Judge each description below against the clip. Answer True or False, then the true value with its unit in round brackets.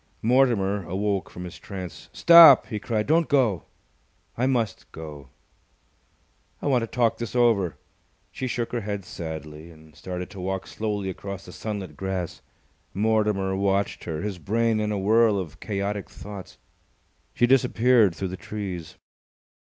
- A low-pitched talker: True (100 Hz)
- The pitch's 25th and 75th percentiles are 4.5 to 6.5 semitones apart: False (3.7 semitones)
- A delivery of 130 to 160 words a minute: True (150 wpm)